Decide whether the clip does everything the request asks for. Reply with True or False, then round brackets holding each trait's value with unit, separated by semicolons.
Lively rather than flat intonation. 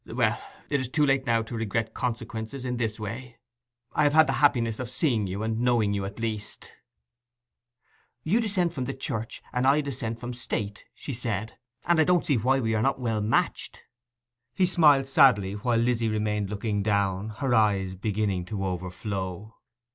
False (3.9 semitones)